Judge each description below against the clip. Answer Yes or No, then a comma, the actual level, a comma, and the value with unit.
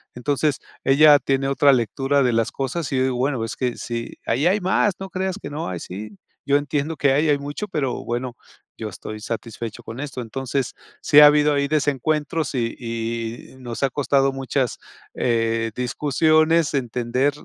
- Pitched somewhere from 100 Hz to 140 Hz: Yes, low, 135 Hz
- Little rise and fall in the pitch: No, average, 3.6 semitones